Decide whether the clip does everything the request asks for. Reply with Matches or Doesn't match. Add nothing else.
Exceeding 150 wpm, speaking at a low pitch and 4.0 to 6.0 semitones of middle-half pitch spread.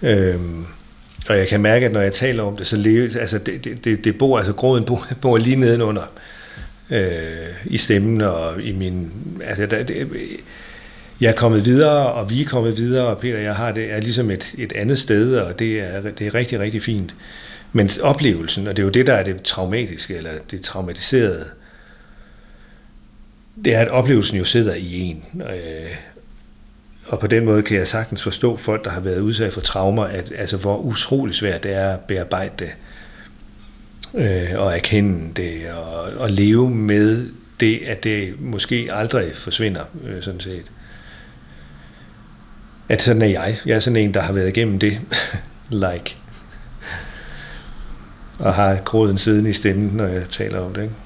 Doesn't match